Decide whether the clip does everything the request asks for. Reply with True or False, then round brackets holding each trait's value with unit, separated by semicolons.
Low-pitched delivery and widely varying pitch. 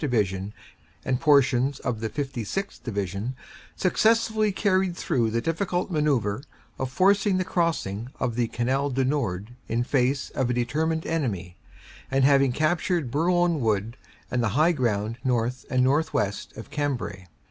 True (130 Hz; 5.7 semitones)